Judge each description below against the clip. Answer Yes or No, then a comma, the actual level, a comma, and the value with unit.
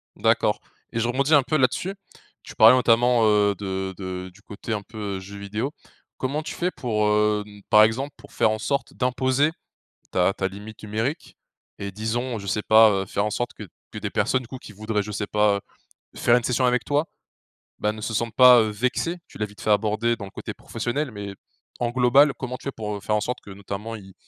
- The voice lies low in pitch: Yes, low, 110 Hz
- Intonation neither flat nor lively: Yes, average, 3.3 semitones